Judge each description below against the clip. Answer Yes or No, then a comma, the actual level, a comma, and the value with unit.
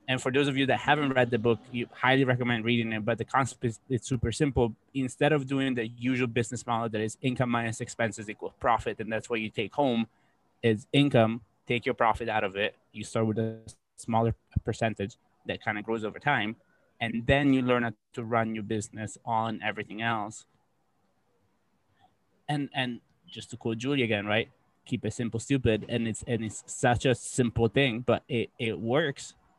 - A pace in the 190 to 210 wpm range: Yes, average, 200 wpm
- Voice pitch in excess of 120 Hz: No, low, 115 Hz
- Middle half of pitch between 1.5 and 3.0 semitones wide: Yes, narrow, 2.4 semitones